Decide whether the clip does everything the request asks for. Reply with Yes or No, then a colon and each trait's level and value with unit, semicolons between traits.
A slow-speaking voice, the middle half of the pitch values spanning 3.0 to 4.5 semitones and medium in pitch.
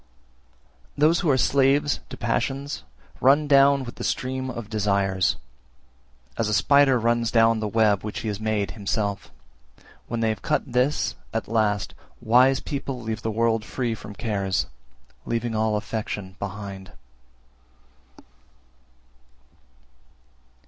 No: slow, 130 wpm; average, 3.9 semitones; low, 115 Hz